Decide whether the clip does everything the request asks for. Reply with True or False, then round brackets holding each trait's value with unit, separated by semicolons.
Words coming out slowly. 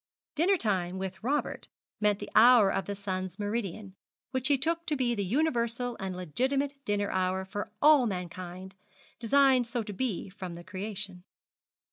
False (160 wpm)